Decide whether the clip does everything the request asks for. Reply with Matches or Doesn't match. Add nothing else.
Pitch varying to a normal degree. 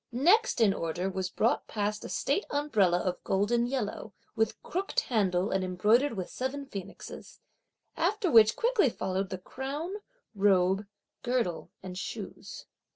Doesn't match